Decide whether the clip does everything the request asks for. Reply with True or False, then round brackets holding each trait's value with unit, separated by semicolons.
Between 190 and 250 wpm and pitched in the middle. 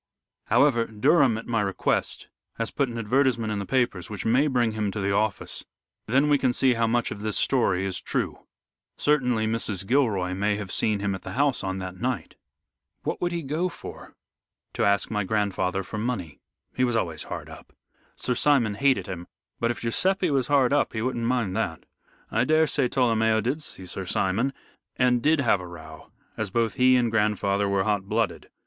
False (195 wpm; 115 Hz)